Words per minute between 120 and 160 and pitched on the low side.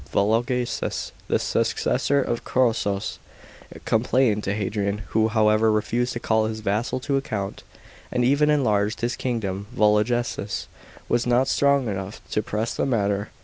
Yes: average, 145 wpm; low, 110 Hz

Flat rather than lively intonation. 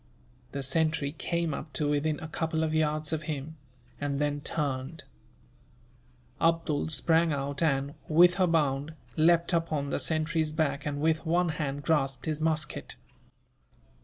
Yes: narrow, 2.1 semitones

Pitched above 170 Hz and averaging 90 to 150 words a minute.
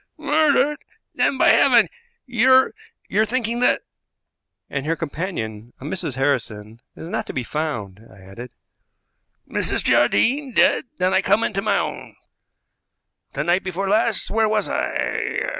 Yes: medium, 185 Hz; average, 145 wpm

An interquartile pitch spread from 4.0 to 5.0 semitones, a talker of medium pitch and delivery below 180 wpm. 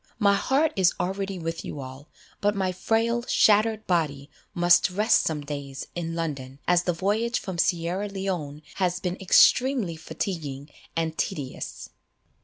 Yes: average, 4.3 semitones; medium, 180 Hz; average, 145 wpm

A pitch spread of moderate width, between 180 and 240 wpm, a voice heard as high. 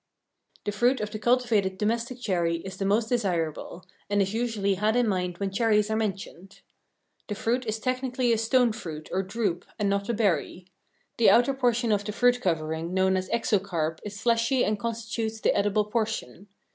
Yes: average, 3.5 semitones; average, 185 wpm; high, 210 Hz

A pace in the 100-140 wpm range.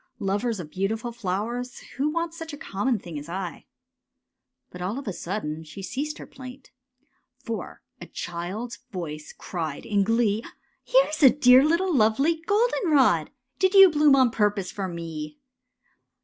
No: average, 160 wpm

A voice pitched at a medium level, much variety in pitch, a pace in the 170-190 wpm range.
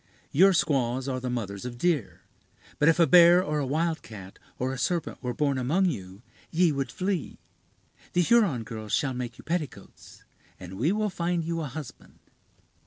Yes: medium, 145 Hz; wide, 5.8 semitones; average, 175 wpm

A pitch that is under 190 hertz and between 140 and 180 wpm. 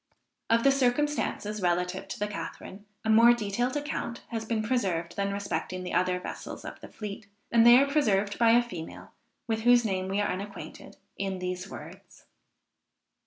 No: high, 210 Hz; average, 170 wpm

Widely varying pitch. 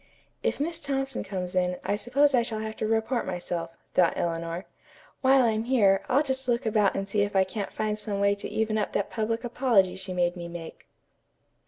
No: average, 4.3 semitones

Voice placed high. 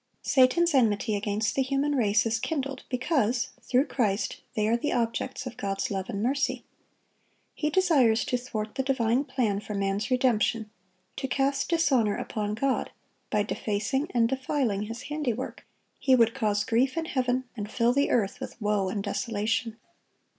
Yes: high, 240 Hz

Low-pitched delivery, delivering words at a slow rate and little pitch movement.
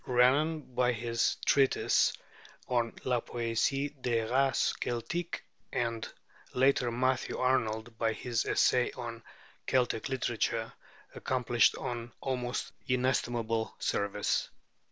Yes: low, 120 Hz; slow, 100 wpm; narrow, 2.0 semitones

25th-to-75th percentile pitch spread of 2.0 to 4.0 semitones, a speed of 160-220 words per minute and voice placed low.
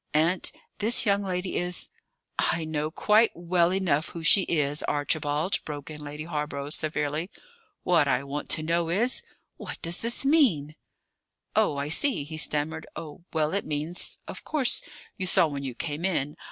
No: average, 3.4 semitones; average, 170 wpm; medium, 160 Hz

